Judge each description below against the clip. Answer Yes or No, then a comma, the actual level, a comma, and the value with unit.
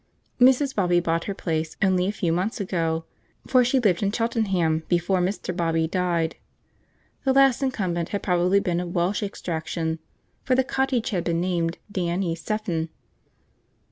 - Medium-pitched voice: Yes, medium, 180 Hz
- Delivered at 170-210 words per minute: No, average, 160 wpm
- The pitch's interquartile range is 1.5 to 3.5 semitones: No, average, 3.9 semitones